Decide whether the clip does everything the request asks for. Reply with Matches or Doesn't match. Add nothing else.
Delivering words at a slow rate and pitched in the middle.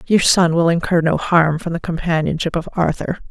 Doesn't match